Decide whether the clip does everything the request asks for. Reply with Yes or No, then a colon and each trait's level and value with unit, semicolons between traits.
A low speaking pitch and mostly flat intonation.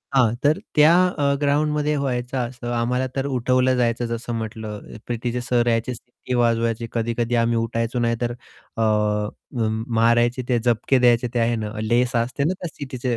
Yes: low, 120 Hz; narrow, 1.7 semitones